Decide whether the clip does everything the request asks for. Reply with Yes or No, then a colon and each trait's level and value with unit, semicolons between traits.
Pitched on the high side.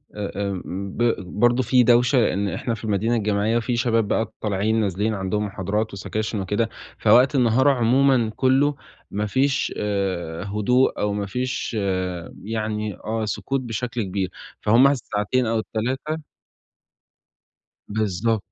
No: low, 110 Hz